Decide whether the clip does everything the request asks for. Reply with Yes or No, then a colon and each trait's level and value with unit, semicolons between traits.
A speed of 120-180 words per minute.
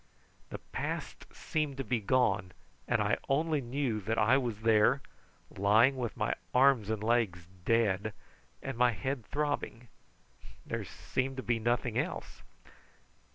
Yes: average, 140 wpm